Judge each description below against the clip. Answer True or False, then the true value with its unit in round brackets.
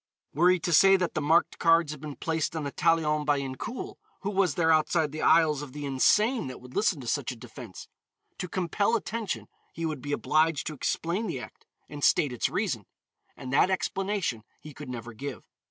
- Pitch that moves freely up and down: False (4.0 semitones)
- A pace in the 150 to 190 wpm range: False (205 wpm)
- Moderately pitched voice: True (155 Hz)